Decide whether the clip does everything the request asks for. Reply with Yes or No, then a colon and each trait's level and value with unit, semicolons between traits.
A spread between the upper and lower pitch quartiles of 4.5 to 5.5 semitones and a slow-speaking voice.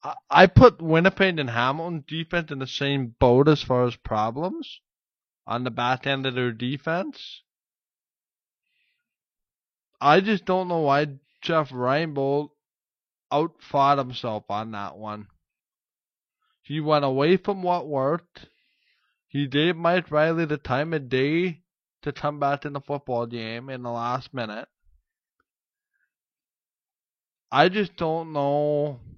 Yes: average, 4.9 semitones; slow, 130 wpm